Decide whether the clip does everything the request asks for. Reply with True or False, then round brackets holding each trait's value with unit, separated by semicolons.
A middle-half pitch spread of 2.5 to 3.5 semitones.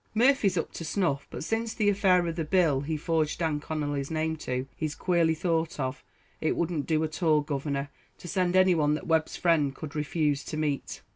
True (3.0 semitones)